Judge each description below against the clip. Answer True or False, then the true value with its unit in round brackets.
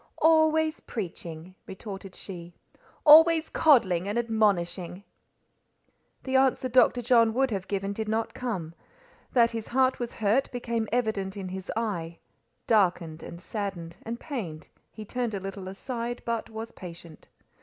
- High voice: True (220 Hz)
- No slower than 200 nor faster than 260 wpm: False (140 wpm)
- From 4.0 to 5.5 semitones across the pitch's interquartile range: True (4.6 semitones)